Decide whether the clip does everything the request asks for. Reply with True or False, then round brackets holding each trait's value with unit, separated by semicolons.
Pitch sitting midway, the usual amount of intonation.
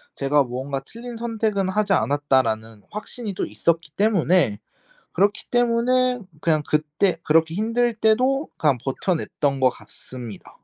False (180 Hz; 8.4 semitones)